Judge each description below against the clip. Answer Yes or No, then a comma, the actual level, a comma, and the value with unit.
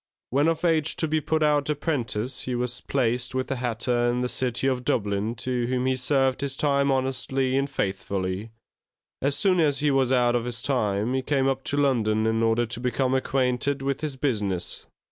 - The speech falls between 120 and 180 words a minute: No, average, 200 wpm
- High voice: No, low, 130 Hz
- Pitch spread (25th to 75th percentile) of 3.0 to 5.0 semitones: No, narrow, 2.6 semitones